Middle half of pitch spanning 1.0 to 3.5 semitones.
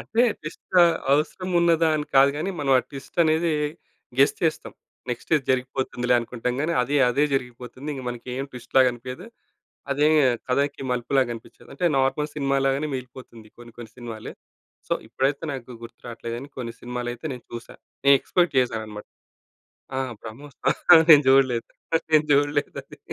Yes: average, 3.1 semitones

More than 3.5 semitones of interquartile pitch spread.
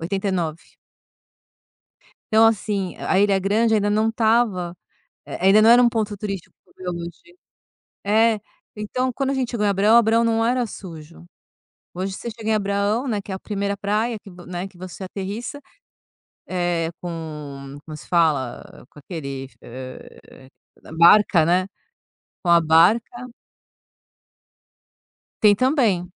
Yes: average, 4.6 semitones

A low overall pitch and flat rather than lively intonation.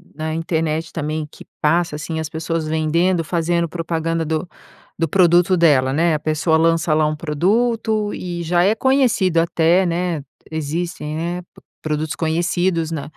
No: medium, 165 Hz; narrow, 1.9 semitones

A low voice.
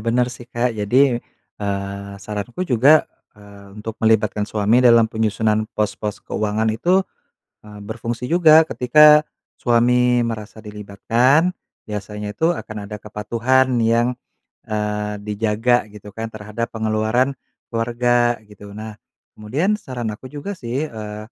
Yes: low, 110 Hz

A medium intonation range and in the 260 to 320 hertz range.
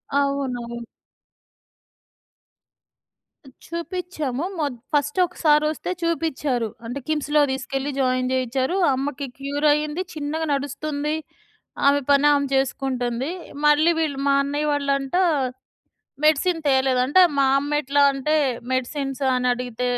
No: narrow, 2.3 semitones; very high, 280 Hz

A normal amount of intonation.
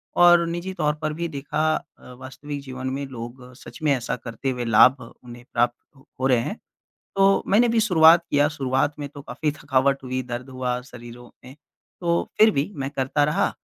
Yes: average, 3.8 semitones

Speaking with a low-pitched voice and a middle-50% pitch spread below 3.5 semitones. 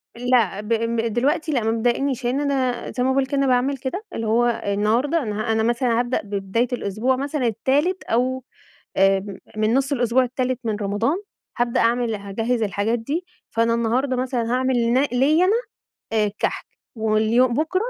No: high, 240 Hz; average, 2.8 semitones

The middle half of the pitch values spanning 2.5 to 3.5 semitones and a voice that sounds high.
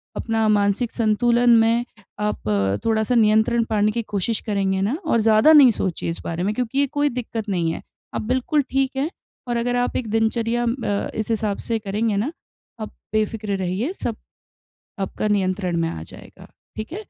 Yes: average, 2.8 semitones; high, 220 Hz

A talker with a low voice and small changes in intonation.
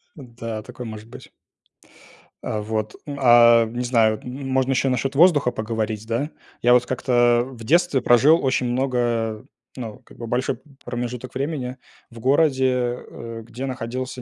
Yes: low, 125 Hz; narrow, 2.3 semitones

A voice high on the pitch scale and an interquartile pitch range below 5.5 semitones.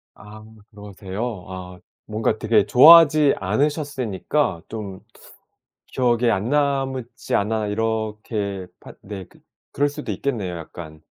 No: low, 110 Hz; average, 5.1 semitones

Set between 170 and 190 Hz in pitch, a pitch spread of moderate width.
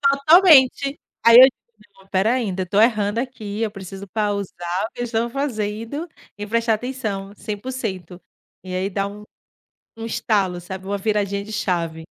No: high, 210 Hz; average, 3.4 semitones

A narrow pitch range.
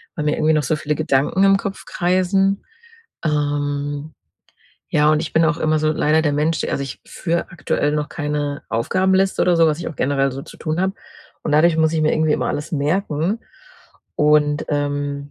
Yes: narrow, 2.3 semitones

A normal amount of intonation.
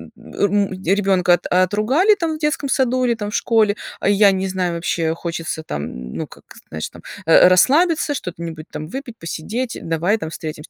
No: wide, 6.1 semitones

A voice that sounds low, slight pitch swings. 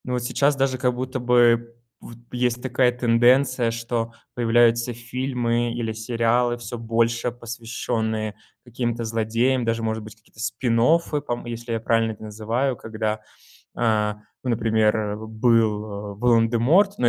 Yes: low, 115 Hz; narrow, 1.6 semitones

